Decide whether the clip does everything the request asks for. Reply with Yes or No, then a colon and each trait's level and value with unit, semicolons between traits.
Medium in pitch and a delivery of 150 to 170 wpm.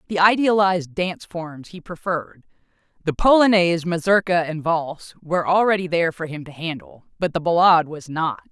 Yes: medium, 170 Hz; average, 160 wpm